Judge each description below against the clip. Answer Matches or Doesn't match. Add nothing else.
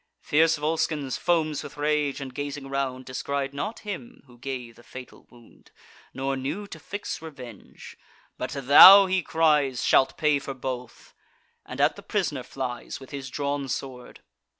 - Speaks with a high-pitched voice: Doesn't match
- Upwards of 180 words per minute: Doesn't match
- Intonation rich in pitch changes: Doesn't match